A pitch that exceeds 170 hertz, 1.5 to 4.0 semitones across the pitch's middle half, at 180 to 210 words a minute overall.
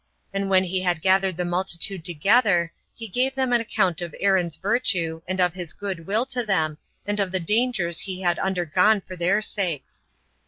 Yes: high, 190 Hz; average, 2.9 semitones; average, 190 wpm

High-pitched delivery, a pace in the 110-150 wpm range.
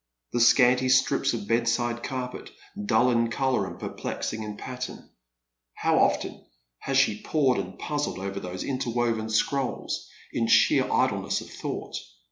No: low, 120 Hz; average, 140 wpm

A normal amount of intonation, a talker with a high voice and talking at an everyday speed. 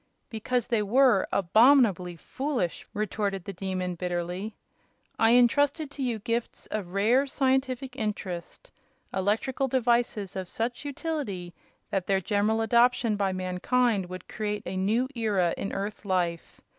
No: average, 4.7 semitones; high, 215 Hz; slow, 130 wpm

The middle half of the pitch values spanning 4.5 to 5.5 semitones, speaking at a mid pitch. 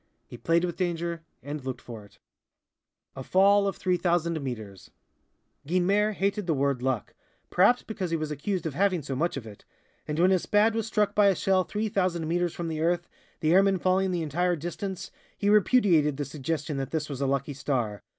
Yes: average, 5.1 semitones; medium, 170 Hz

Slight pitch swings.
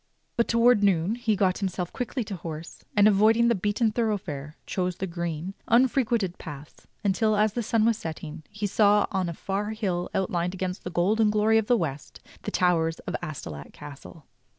No: average, 4.1 semitones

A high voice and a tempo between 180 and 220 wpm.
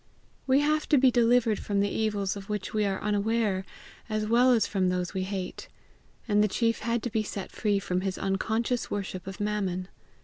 Yes: high, 210 Hz; average, 200 wpm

